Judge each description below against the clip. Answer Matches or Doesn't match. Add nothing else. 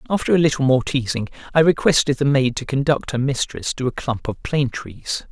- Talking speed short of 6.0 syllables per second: Matches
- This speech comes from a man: Matches